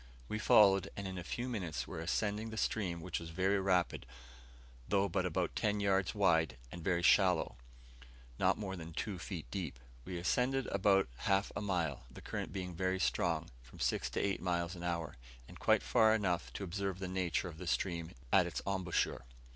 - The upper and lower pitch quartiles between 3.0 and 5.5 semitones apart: No, narrow, 2.5 semitones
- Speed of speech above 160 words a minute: Yes, average, 190 wpm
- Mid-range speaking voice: No, very low, 95 Hz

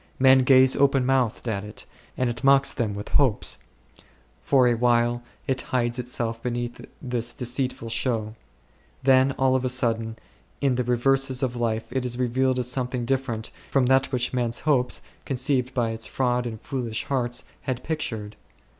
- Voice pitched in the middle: No, low, 125 Hz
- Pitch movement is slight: Yes, narrow, 1.9 semitones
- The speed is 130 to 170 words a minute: Yes, average, 165 wpm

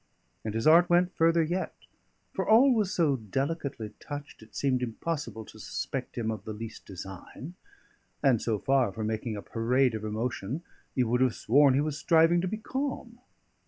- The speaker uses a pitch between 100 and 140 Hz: Yes, low, 135 Hz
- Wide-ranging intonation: Yes, wide, 6.9 semitones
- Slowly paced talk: No, average, 180 wpm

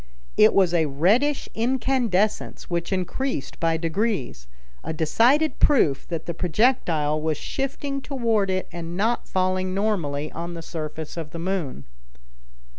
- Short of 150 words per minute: Yes, slow, 135 wpm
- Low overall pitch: No, medium, 185 Hz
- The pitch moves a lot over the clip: Yes, wide, 6.0 semitones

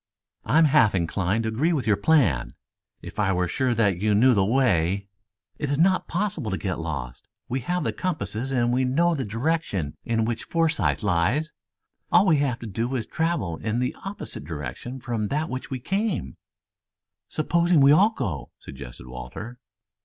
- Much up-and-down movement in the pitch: Yes, wide, 7.7 semitones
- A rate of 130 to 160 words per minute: No, average, 190 wpm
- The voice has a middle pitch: No, low, 120 Hz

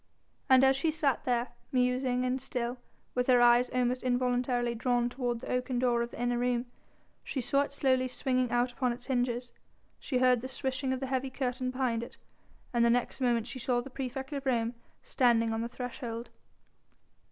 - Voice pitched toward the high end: Yes, very high, 250 Hz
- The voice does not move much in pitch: Yes, narrow, 1.2 semitones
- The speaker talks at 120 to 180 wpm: No, average, 190 wpm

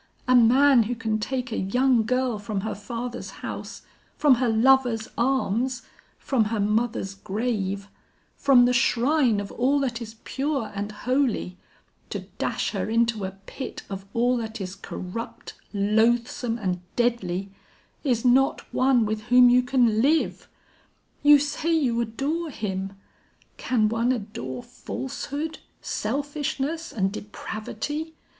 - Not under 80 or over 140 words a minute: Yes, slow, 135 wpm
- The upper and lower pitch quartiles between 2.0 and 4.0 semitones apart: Yes, average, 3.7 semitones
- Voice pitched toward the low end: No, high, 235 Hz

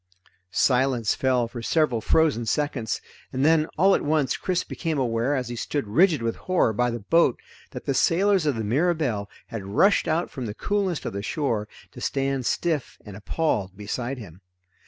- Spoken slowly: No, average, 180 wpm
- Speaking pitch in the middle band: No, low, 130 Hz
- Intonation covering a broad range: Yes, wide, 5.8 semitones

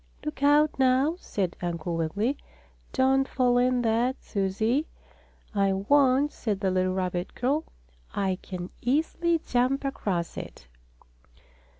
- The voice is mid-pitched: No, high, 245 Hz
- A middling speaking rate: No, slow, 120 wpm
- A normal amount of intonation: No, wide, 6.2 semitones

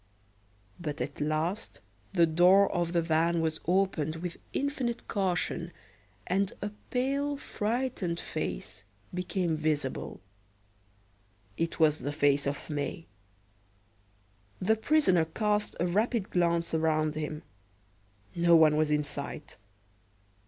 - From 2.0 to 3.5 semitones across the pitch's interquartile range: No, average, 4.1 semitones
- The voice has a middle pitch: Yes, medium, 170 Hz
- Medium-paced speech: No, slow, 115 wpm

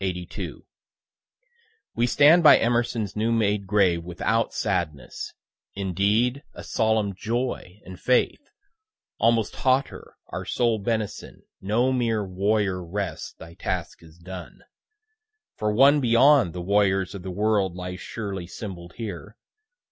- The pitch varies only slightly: No, average, 4.0 semitones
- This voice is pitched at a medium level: No, low, 105 Hz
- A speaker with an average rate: No, slow, 125 wpm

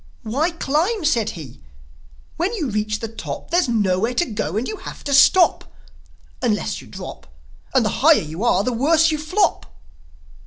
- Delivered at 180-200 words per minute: No, average, 170 wpm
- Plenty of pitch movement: Yes, wide, 7.4 semitones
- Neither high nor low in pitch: No, very high, 250 Hz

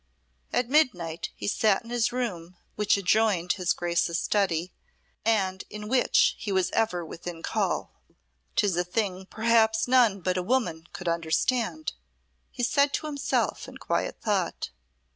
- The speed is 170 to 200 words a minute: No, average, 145 wpm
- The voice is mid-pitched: No, high, 200 Hz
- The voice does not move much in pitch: No, average, 4.7 semitones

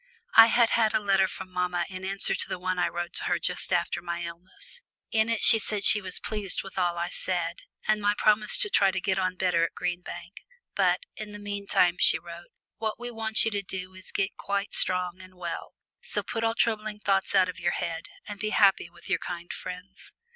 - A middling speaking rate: No, fast, 230 wpm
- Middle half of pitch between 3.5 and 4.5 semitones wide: No, average, 2.9 semitones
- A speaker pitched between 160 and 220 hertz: Yes, high, 190 Hz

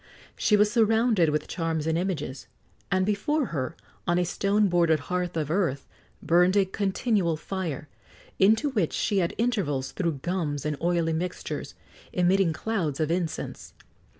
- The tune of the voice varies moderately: Yes, average, 3.9 semitones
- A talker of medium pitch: Yes, medium, 180 Hz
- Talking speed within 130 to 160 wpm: Yes, average, 150 wpm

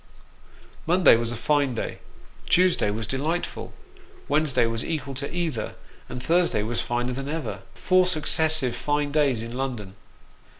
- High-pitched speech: No, low, 135 Hz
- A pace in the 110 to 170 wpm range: Yes, average, 140 wpm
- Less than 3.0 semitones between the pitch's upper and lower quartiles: No, average, 4.9 semitones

